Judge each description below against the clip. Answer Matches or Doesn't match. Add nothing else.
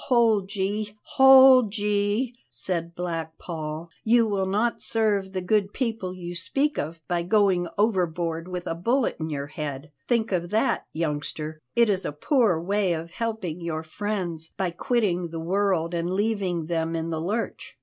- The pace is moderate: Matches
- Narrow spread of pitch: Doesn't match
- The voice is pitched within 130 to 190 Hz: Matches